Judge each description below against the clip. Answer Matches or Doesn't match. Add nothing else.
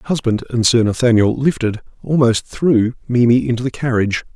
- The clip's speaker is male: Matches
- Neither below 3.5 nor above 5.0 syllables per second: Doesn't match